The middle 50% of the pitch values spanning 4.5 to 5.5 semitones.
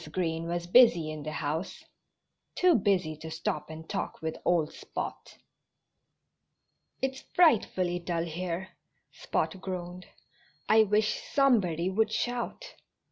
Yes: average, 4.8 semitones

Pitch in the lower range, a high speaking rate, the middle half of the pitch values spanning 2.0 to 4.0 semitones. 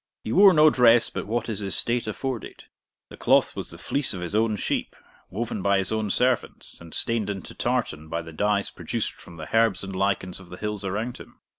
Yes: low, 105 Hz; fast, 210 wpm; average, 3.5 semitones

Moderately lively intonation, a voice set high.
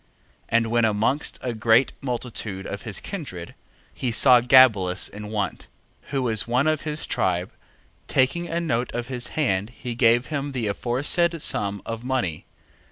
No: average, 4.1 semitones; low, 120 Hz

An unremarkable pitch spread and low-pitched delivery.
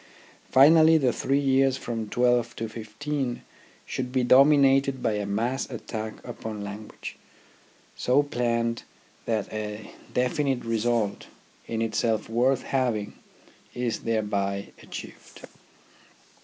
Yes: average, 3.4 semitones; low, 120 Hz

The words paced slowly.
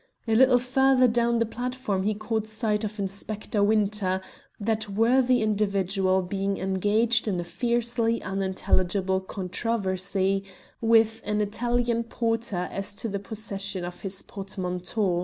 Yes: slow, 130 wpm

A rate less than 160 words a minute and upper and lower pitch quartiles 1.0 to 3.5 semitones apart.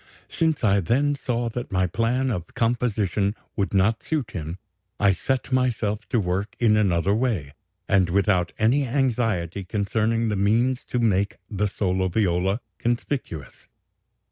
No: average, 140 wpm; average, 4.1 semitones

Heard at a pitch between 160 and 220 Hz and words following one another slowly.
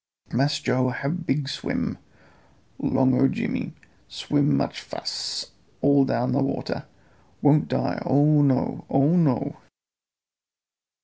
No: medium, 140 Hz; slow, 115 wpm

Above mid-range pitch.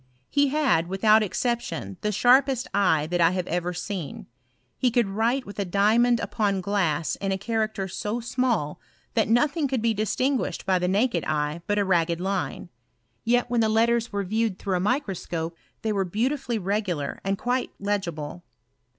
Yes: high, 205 Hz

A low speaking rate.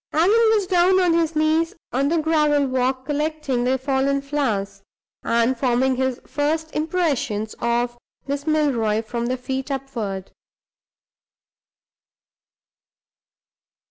Yes: slow, 110 wpm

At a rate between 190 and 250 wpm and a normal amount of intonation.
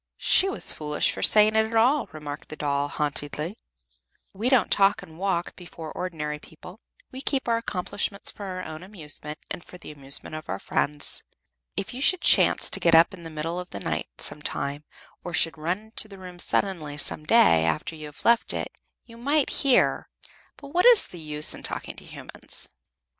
No: average, 200 wpm; wide, 6.3 semitones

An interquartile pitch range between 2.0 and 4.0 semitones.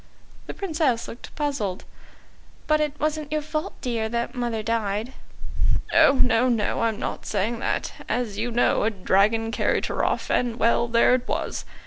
Yes: average, 3.7 semitones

